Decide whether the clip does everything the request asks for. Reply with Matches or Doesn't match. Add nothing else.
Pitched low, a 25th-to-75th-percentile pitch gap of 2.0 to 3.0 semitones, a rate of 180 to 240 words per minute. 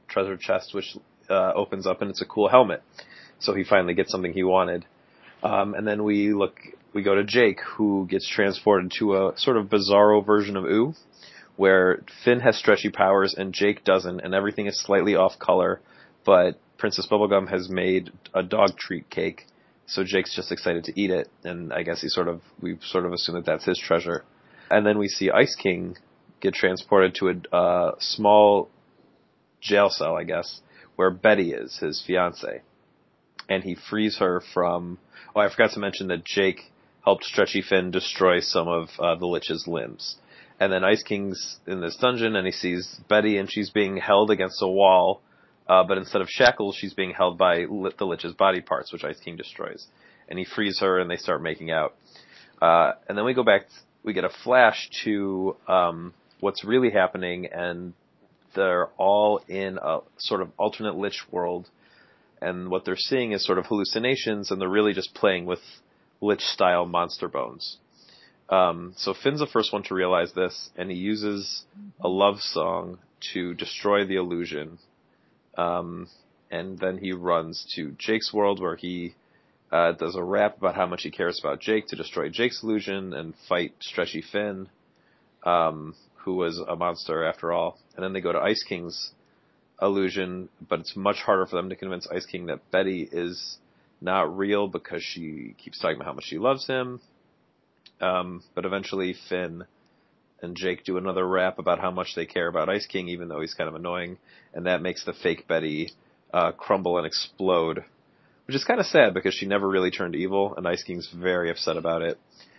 Matches